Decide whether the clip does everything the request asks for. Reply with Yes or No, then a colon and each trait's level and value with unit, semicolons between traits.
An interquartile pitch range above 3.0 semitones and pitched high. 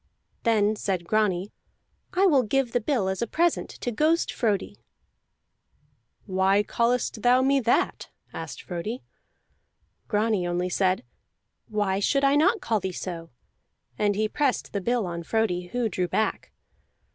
Yes: average, 4.6 semitones; high, 215 Hz